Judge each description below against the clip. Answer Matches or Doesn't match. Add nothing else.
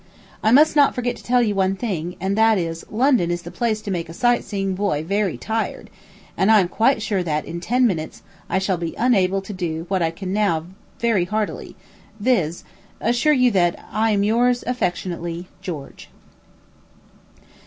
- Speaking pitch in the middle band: Doesn't match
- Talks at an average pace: Matches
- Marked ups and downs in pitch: Doesn't match